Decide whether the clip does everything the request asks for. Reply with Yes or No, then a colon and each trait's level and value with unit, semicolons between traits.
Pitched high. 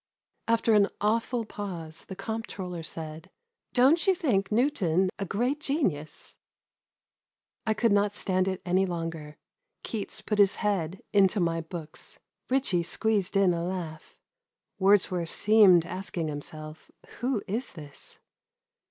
Yes: high, 195 Hz